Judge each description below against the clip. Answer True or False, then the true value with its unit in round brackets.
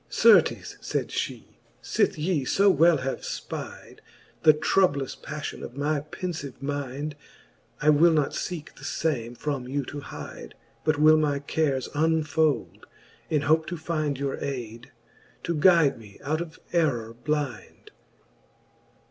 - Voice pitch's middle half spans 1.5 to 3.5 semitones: True (2.6 semitones)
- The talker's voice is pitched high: False (150 Hz)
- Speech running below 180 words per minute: True (140 wpm)